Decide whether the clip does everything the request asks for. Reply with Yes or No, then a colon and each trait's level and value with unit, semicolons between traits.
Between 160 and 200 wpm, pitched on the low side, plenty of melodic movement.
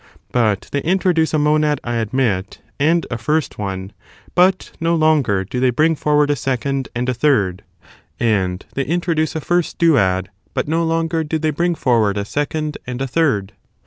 No: average, 175 wpm; medium, 145 Hz; wide, 5.7 semitones